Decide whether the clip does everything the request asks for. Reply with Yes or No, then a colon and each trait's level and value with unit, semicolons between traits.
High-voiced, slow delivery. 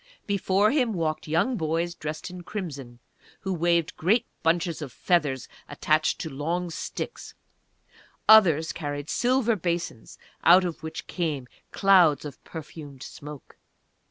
No: medium, 165 Hz; slow, 130 wpm